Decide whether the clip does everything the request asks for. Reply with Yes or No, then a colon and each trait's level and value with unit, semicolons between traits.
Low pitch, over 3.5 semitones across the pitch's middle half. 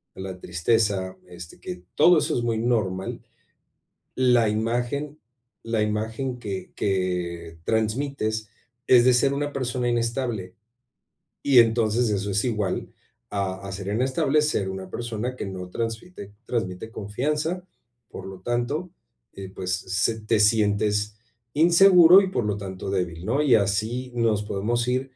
Yes: low, 110 Hz; average, 4.2 semitones